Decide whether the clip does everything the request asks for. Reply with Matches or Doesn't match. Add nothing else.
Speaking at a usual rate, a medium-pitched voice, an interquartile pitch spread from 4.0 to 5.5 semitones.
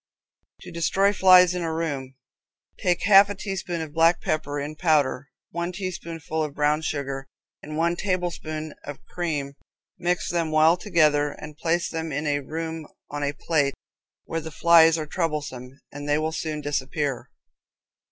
Doesn't match